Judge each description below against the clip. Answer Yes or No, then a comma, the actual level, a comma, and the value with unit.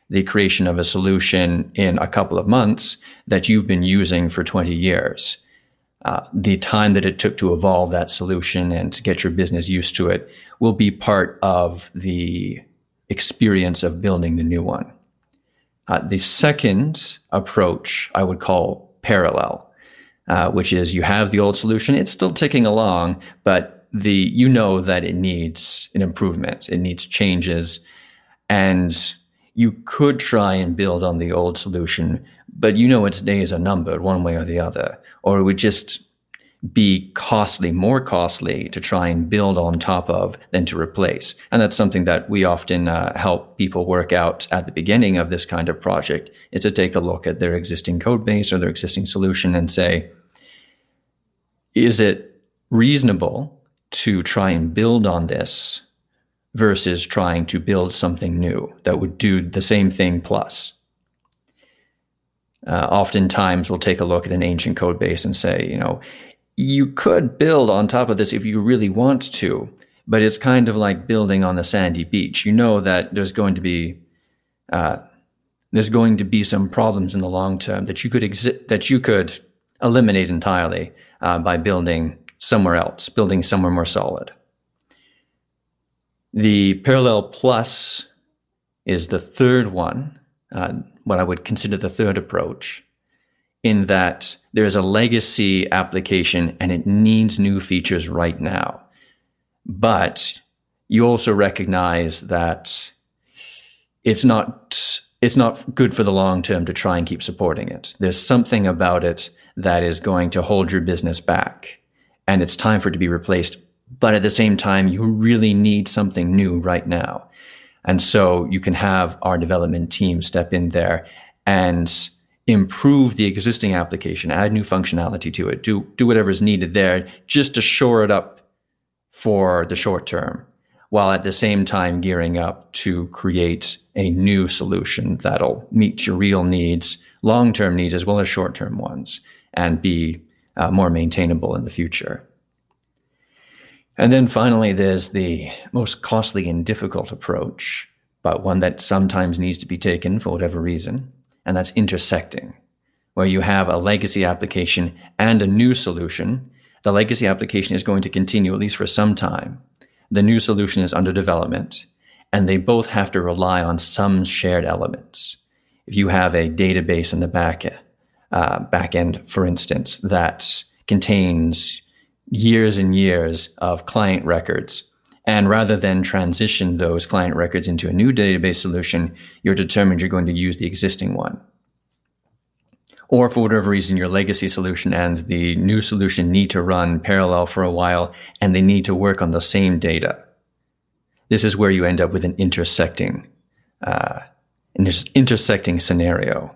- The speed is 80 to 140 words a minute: No, average, 165 wpm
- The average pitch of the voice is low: Yes, very low, 95 Hz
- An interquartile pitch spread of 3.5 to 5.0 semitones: No, average, 2.9 semitones